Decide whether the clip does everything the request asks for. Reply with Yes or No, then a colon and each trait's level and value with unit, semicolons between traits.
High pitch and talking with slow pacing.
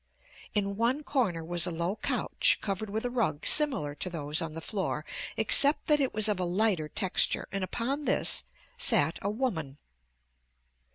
No: high, 195 Hz; average, 170 wpm